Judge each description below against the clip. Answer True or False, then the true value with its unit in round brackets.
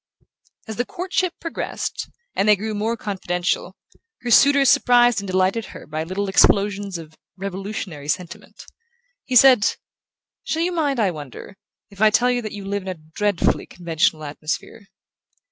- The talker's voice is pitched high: True (200 Hz)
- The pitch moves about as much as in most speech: True (4.9 semitones)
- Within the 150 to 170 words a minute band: True (160 wpm)